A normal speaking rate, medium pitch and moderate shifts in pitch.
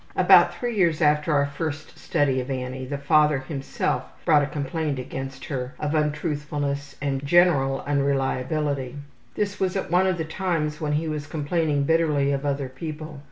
No: average, 165 wpm; medium, 145 Hz; narrow, 2.3 semitones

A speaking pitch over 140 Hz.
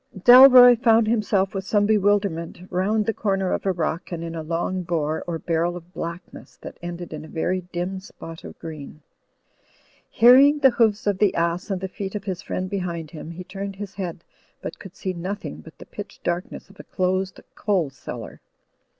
Yes: medium, 185 Hz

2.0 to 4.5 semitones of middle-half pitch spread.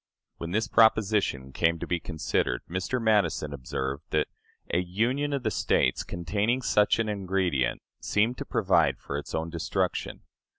No: wide, 5.5 semitones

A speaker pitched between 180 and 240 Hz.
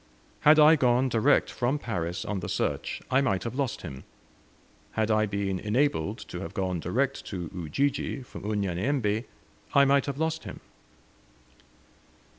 No: low, 115 Hz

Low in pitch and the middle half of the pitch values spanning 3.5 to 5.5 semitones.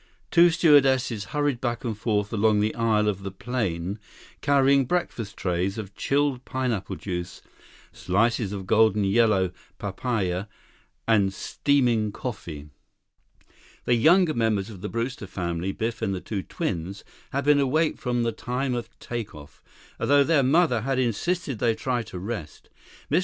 Yes: low, 115 Hz; average, 4.9 semitones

